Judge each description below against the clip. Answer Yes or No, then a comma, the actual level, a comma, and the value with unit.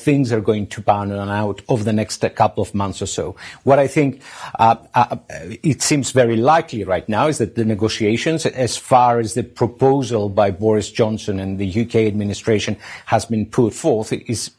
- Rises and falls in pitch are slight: No, average, 3.2 semitones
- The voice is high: No, low, 115 Hz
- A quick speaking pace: No, average, 195 wpm